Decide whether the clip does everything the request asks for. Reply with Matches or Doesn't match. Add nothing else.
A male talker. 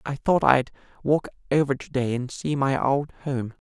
Matches